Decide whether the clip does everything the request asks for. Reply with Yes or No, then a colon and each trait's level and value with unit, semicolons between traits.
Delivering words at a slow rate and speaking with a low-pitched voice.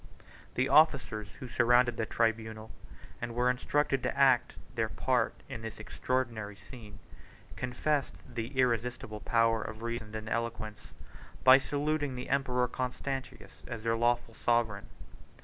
Yes: slow, 130 wpm; low, 120 Hz